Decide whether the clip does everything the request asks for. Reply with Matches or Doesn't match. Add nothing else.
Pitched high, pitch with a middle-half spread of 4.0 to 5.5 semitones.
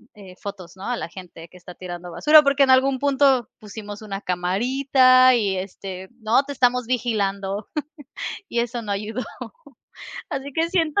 Matches